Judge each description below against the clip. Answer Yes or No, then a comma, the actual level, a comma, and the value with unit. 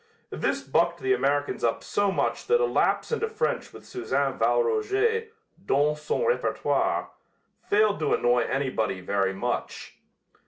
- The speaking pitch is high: Yes, high, 200 Hz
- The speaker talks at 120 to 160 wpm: Yes, average, 140 wpm